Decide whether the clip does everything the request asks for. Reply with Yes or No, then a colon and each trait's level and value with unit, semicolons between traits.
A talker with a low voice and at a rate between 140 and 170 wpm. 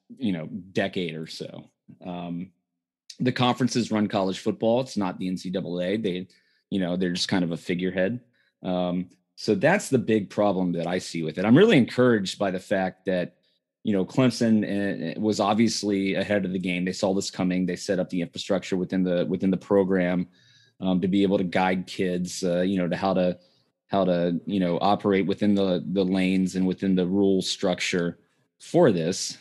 No: very low, 95 Hz; average, 190 wpm